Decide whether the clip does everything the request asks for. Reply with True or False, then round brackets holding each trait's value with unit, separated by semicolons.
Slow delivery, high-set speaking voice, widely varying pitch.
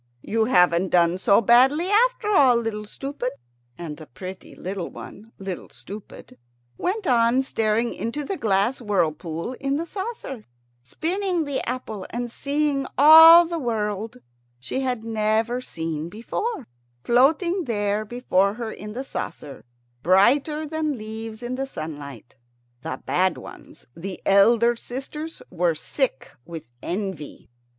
True (130 wpm; 230 Hz; 6.4 semitones)